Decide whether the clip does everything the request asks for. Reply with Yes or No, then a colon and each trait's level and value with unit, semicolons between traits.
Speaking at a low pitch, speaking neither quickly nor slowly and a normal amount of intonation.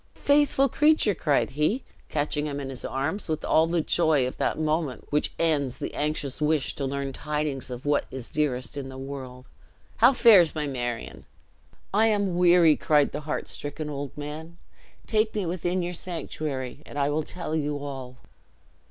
No: medium, 150 Hz; average, 175 wpm; average, 3.6 semitones